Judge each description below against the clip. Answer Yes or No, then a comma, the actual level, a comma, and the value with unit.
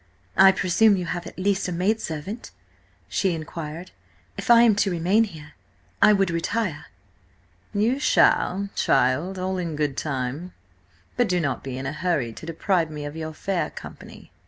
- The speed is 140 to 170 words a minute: Yes, average, 165 wpm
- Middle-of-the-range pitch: Yes, medium, 175 Hz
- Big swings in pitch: No, average, 4.2 semitones